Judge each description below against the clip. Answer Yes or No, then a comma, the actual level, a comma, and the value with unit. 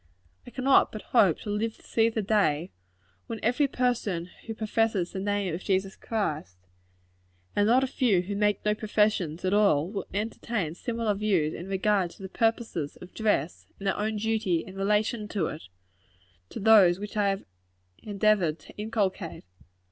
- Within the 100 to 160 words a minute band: No, average, 170 wpm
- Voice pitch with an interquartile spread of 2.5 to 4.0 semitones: Yes, average, 2.9 semitones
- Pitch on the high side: Yes, high, 205 Hz